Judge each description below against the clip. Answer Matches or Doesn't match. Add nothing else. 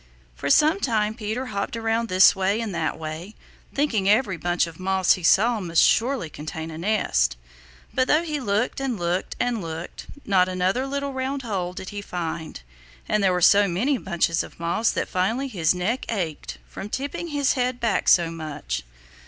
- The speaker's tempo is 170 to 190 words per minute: Matches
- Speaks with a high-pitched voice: Matches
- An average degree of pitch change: Doesn't match